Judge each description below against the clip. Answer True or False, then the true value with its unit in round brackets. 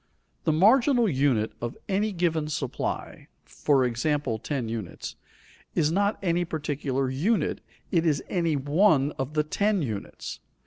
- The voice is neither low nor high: True (150 Hz)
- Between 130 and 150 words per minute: True (135 wpm)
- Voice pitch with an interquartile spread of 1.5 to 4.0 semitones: False (5.0 semitones)